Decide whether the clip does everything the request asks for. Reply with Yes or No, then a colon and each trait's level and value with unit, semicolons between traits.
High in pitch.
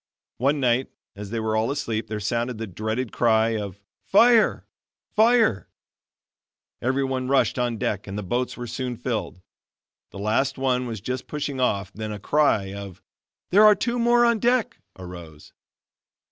No: low, 120 Hz